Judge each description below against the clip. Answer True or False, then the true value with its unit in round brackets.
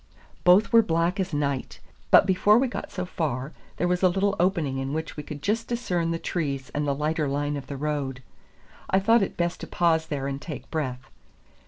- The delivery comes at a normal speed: False (210 wpm)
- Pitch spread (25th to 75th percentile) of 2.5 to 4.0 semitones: False (4.5 semitones)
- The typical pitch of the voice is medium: True (160 Hz)